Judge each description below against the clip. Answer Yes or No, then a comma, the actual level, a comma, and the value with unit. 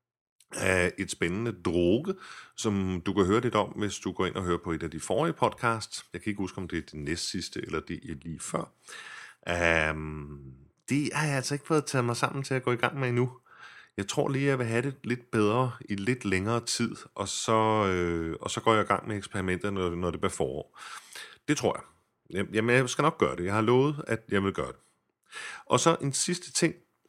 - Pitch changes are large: Yes, wide, 5.8 semitones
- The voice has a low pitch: Yes, low, 110 Hz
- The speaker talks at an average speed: No, fast, 235 wpm